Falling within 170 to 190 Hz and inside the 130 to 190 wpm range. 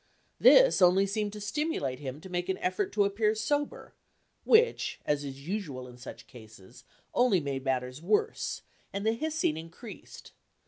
Yes: medium, 185 Hz; average, 155 wpm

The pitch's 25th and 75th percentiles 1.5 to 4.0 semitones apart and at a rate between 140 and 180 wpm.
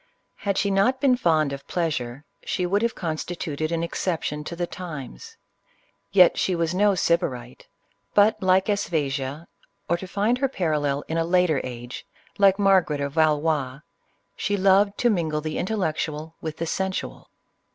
No: average, 4.4 semitones; average, 165 wpm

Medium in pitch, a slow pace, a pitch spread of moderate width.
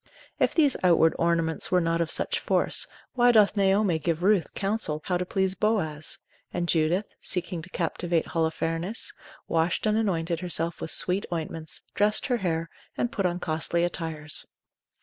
No: medium, 175 Hz; average, 160 wpm; average, 3.3 semitones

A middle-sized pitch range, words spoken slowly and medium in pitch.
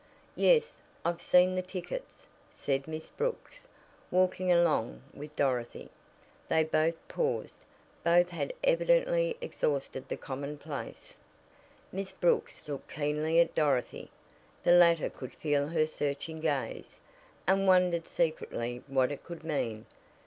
Yes: average, 4.3 semitones; slow, 120 wpm; medium, 165 Hz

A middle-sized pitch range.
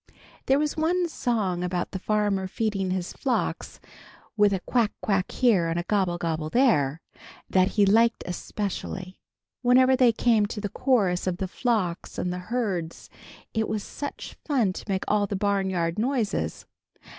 Yes: average, 4.4 semitones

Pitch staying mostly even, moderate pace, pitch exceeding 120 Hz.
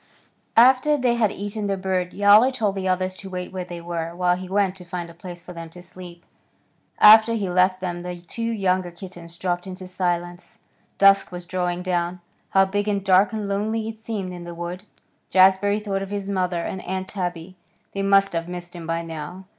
No: narrow, 2.2 semitones; fast, 210 wpm; medium, 185 Hz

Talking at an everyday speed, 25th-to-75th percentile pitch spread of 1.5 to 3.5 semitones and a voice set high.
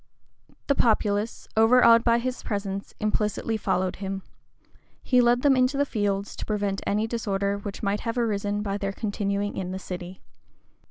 Yes: average, 160 wpm; average, 2.7 semitones; high, 205 Hz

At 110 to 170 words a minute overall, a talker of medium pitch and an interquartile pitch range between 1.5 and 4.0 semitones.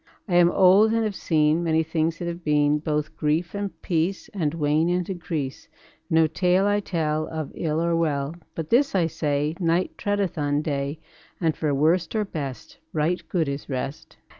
No: average, 185 wpm; medium, 160 Hz; average, 3.0 semitones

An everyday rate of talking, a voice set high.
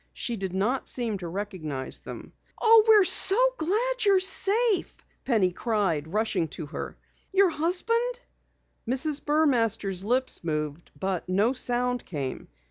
No: slow, 130 wpm; high, 240 Hz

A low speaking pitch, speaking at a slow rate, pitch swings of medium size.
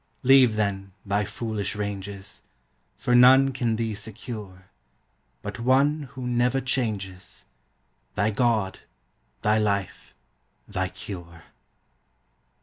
Yes: low, 110 Hz; slow, 100 wpm; average, 3.9 semitones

